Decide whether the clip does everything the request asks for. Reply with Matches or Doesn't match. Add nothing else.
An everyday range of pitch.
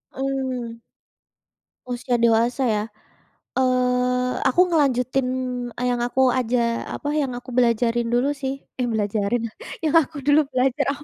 Doesn't match